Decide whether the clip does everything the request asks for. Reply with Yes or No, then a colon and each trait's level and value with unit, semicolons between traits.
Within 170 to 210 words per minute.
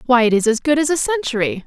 No: fast, 290 wpm